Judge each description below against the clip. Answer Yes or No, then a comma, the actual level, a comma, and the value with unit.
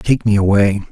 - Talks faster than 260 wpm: No, average, 200 wpm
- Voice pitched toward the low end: Yes, low, 105 Hz